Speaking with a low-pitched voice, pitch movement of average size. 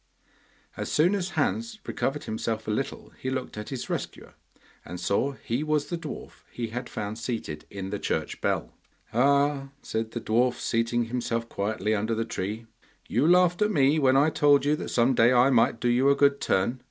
Yes: low, 125 Hz; average, 4.0 semitones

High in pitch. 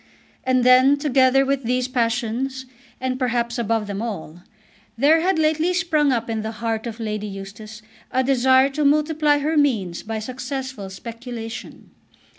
Yes: very high, 250 Hz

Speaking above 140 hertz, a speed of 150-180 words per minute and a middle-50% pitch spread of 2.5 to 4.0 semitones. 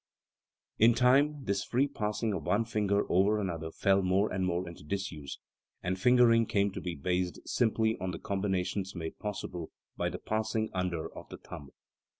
No: low, 100 Hz; average, 175 wpm; average, 3.4 semitones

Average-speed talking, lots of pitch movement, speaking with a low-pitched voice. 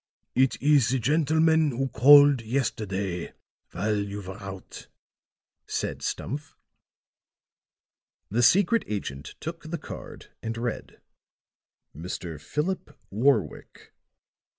No: slow, 100 wpm; wide, 6.7 semitones; low, 120 Hz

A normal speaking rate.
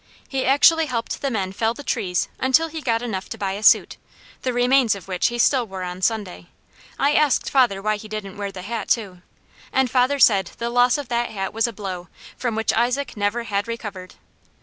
No: fast, 215 wpm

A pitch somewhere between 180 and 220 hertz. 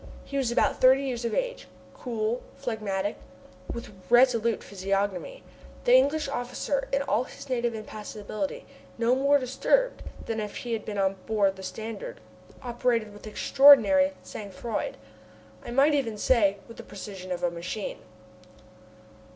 No: high, 235 Hz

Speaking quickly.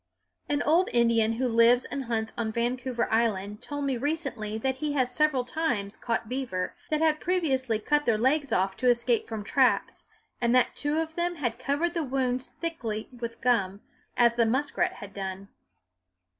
No: average, 175 wpm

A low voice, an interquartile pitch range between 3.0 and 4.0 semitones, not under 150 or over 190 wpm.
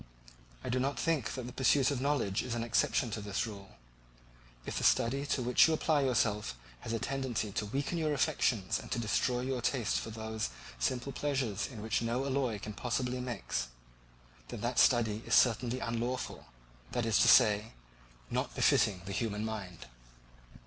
Yes: low, 120 Hz; average, 3.4 semitones; average, 175 wpm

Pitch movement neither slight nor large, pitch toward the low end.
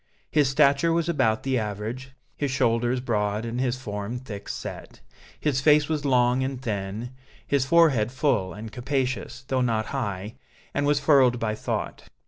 Yes: average, 3.9 semitones; low, 125 Hz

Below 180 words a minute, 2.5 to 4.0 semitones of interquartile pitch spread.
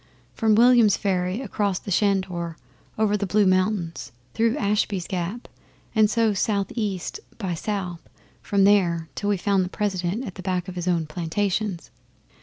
Yes: average, 160 wpm; average, 2.9 semitones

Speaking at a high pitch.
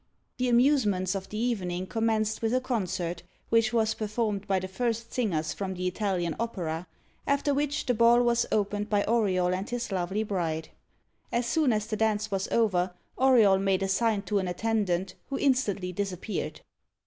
Yes: high, 210 Hz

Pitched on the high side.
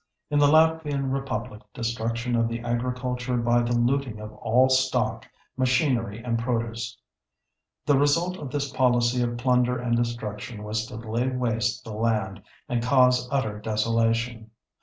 No: low, 120 Hz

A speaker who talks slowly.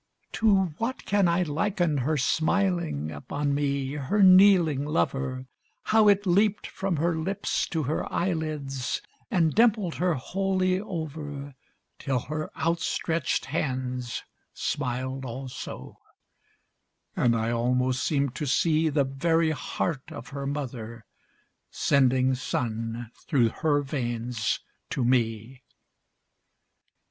Yes: slow, 115 wpm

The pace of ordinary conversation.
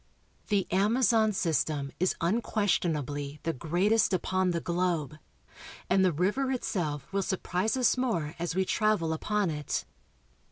No: slow, 130 wpm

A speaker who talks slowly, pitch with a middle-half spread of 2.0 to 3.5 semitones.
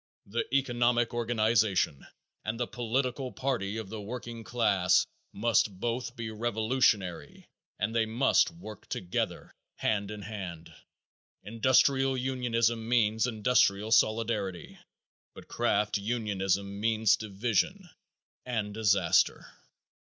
Yes: slow, 105 wpm; average, 2.7 semitones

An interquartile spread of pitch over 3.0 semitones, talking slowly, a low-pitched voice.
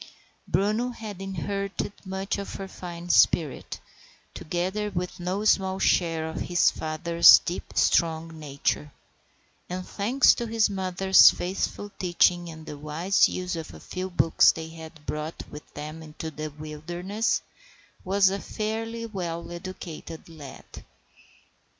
No: average, 3.5 semitones; slow, 130 wpm; medium, 175 Hz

